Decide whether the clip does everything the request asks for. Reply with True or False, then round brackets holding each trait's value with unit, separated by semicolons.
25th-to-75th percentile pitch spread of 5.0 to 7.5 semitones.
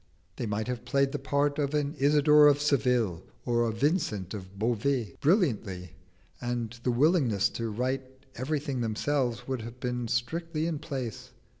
False (4.0 semitones)